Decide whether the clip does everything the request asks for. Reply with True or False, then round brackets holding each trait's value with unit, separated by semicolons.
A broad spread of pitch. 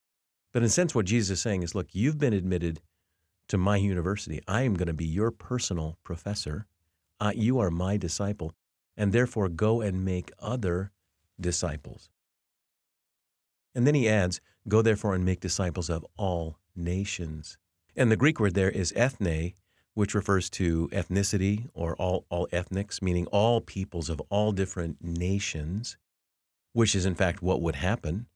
False (3.4 semitones)